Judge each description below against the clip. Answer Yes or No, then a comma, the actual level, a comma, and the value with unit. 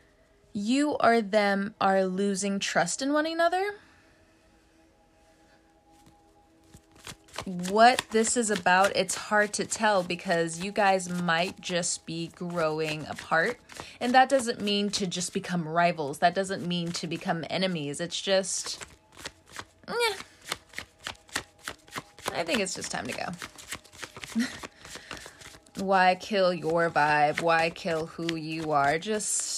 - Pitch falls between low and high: Yes, medium, 180 Hz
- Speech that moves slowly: Yes, slow, 120 wpm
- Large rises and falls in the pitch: No, average, 4.5 semitones